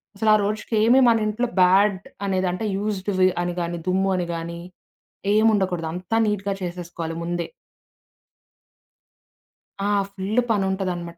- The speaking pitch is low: No, high, 190 Hz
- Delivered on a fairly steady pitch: No, average, 3.2 semitones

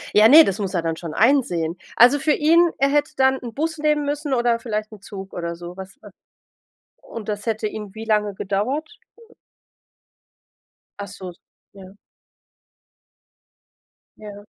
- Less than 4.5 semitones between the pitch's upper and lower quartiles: No, wide, 6.1 semitones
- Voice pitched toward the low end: No, high, 215 Hz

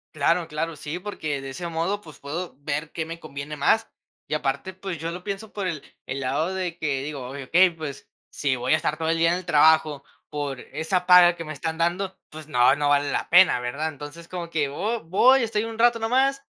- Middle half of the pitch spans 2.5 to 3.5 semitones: No, average, 3.9 semitones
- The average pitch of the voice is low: No, medium, 160 Hz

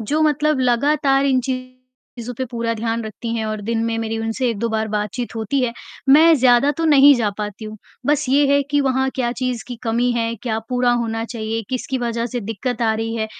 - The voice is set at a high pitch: Yes, high, 240 Hz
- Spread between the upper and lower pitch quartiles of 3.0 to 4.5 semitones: No, narrow, 2.6 semitones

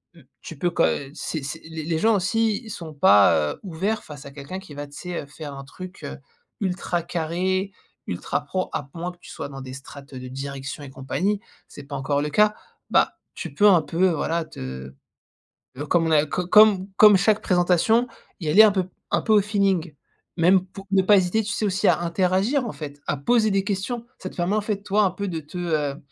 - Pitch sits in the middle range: Yes, medium, 175 Hz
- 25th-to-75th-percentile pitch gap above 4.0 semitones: Yes, average, 5.2 semitones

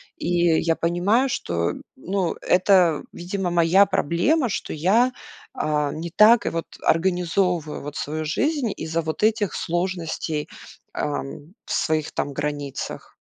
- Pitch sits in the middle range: Yes, medium, 170 Hz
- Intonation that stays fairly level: No, average, 3.7 semitones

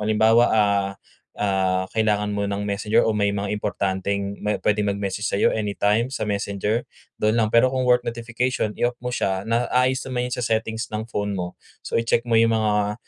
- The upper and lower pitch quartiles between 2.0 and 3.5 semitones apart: Yes, narrow, 2.4 semitones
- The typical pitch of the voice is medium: No, low, 105 Hz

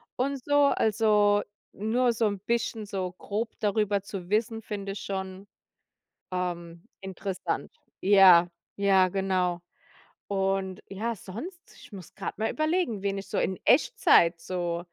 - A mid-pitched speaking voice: No, high, 200 Hz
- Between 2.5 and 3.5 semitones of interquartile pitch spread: Yes, average, 2.9 semitones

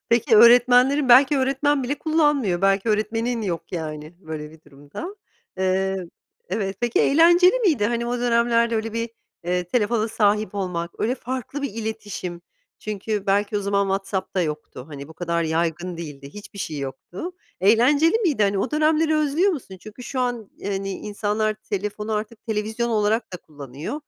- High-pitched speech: Yes, high, 215 Hz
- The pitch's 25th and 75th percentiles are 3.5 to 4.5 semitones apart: No, average, 4.9 semitones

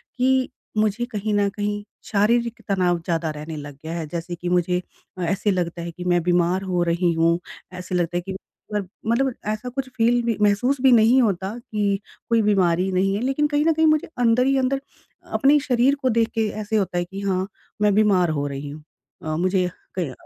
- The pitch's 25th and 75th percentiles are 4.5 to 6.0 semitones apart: Yes, average, 5.0 semitones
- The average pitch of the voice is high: Yes, high, 200 Hz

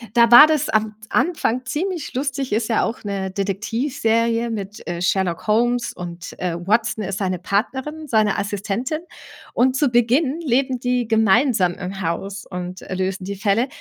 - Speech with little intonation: No, average, 4.6 semitones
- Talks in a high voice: Yes, high, 220 Hz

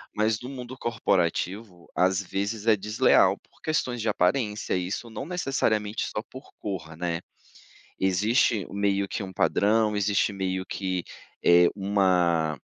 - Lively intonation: No, average, 3.1 semitones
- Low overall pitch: Yes, low, 100 Hz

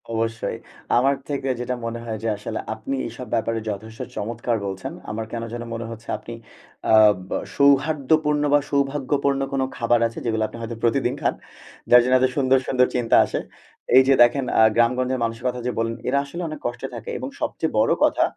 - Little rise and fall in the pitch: No, average, 3.0 semitones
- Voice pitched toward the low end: Yes, low, 120 Hz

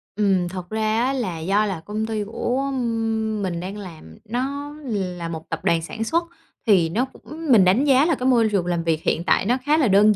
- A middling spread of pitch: No, wide, 5.9 semitones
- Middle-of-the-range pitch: No, high, 210 Hz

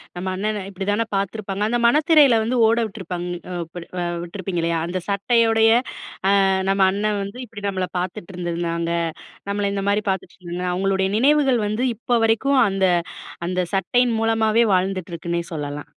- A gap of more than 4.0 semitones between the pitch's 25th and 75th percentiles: No, average, 3.7 semitones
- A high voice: Yes, high, 195 Hz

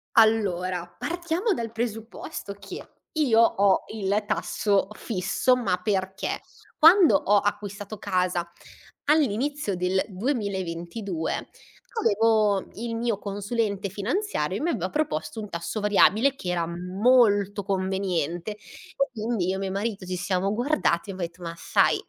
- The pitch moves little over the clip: No, average, 3.7 semitones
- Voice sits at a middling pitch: No, high, 205 Hz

